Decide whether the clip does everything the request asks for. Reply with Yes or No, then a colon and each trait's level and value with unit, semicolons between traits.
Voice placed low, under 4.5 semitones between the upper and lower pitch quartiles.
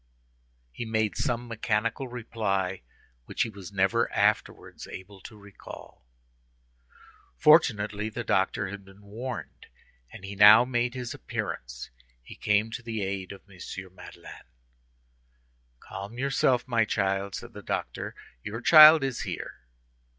Yes: low, 105 Hz; average, 3.5 semitones